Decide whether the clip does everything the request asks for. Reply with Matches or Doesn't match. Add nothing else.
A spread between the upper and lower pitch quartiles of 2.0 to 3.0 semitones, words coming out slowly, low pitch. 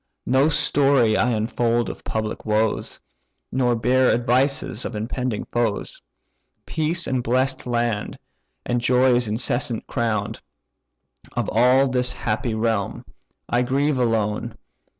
Matches